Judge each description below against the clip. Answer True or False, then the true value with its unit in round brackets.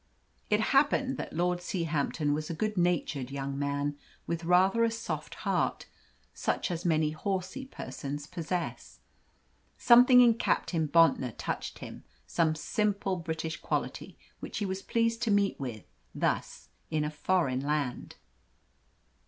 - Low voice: False (170 Hz)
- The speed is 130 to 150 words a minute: True (135 wpm)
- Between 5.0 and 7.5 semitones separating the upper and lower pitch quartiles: True (5.3 semitones)